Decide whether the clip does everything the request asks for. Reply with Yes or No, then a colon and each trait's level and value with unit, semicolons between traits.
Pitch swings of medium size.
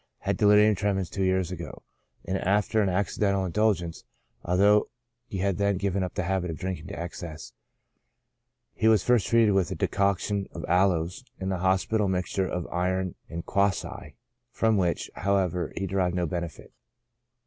No: narrow, 2.0 semitones